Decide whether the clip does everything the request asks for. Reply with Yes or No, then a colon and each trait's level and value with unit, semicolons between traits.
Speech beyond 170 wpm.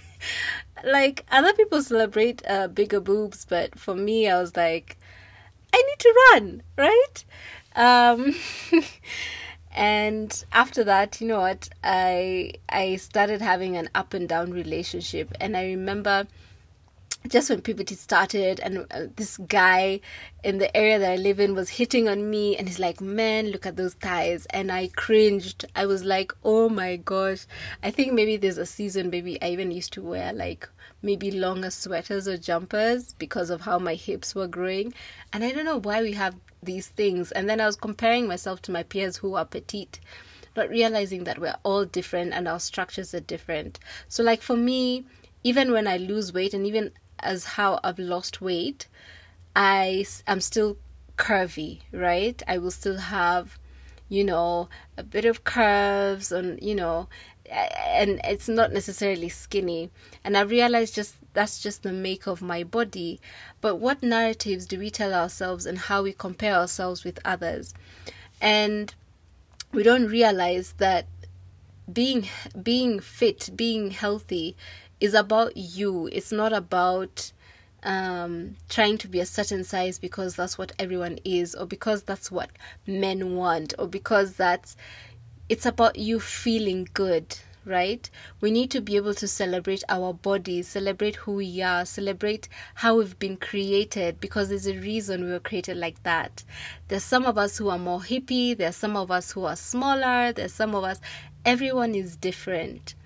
No: average, 165 wpm